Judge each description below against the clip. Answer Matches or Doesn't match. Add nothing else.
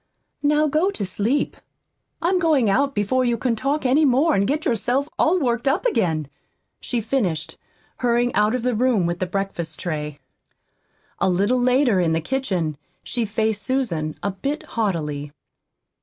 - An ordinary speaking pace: Matches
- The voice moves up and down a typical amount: Doesn't match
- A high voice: Matches